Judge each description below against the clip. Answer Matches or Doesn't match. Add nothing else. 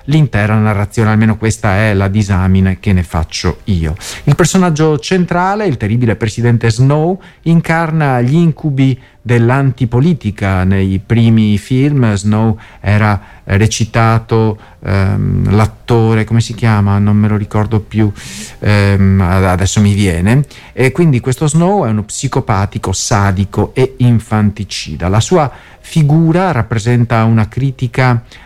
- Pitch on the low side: Matches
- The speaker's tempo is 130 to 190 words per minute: Doesn't match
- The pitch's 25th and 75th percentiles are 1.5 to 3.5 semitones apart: Doesn't match